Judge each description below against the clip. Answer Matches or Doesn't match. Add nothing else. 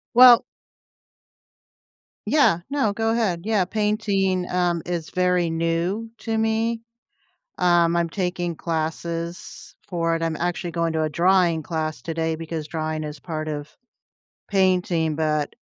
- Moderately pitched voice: Matches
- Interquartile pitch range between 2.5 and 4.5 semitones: Matches